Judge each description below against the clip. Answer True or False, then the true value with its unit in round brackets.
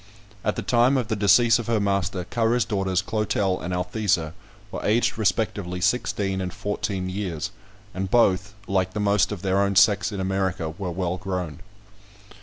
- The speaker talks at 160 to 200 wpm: True (165 wpm)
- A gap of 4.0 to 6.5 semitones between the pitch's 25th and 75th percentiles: False (2.5 semitones)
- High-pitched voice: False (100 Hz)